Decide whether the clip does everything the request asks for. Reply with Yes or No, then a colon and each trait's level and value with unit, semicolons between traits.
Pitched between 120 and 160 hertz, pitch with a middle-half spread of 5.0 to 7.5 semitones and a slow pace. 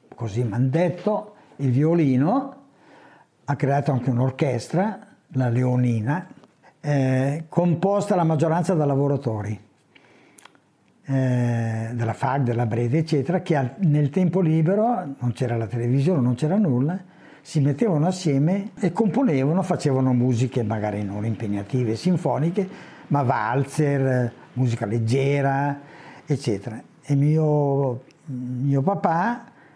Yes: medium, 140 Hz; wide, 5.4 semitones; slow, 110 wpm